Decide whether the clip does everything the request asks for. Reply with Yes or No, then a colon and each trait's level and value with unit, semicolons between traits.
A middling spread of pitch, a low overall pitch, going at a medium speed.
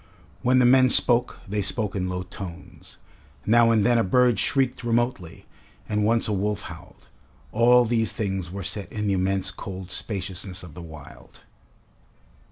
Yes: average, 4.1 semitones; low, 105 Hz; average, 165 wpm